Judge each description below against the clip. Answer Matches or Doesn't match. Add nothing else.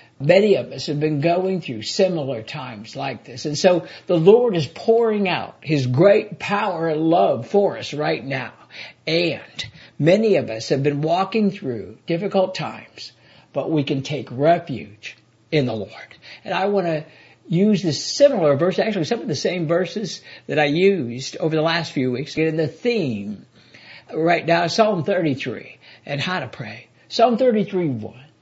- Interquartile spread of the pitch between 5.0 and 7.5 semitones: Matches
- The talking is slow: Doesn't match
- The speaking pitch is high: Doesn't match